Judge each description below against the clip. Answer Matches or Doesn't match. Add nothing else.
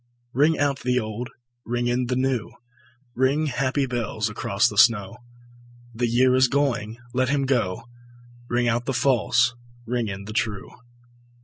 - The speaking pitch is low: Matches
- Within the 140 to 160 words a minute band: Matches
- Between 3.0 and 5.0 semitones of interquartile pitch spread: Doesn't match